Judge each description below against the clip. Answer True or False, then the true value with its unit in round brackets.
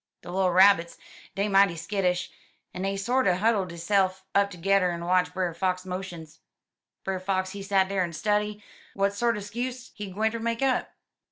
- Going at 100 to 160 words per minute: False (170 wpm)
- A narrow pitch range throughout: True (2.3 semitones)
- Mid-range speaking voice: False (195 Hz)